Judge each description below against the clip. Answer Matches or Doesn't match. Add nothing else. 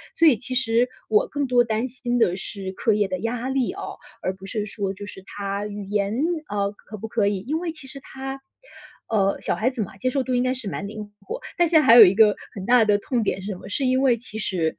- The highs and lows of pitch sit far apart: Doesn't match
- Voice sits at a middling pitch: Doesn't match